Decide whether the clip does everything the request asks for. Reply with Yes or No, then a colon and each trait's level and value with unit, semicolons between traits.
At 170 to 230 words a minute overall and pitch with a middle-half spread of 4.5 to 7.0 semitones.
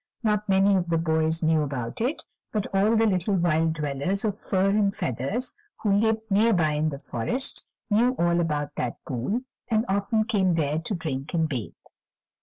Yes: average, 185 wpm; wide, 5.4 semitones